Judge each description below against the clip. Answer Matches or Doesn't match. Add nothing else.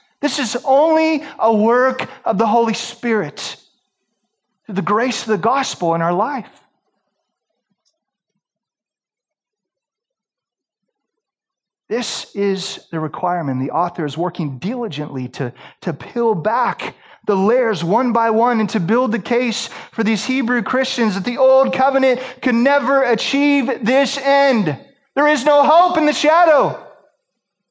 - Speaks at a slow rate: Matches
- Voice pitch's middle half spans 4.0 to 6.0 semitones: Matches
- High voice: Matches